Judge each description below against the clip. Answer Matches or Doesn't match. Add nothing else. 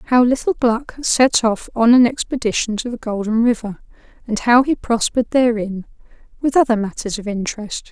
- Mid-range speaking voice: Doesn't match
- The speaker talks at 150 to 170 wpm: Matches